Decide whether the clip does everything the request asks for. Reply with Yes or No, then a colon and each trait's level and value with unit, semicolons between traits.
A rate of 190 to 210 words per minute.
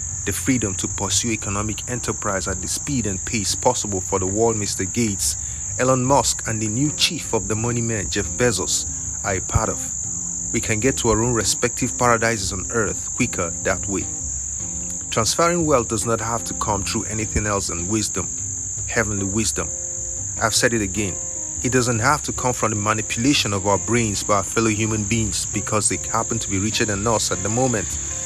Yes: average, 195 wpm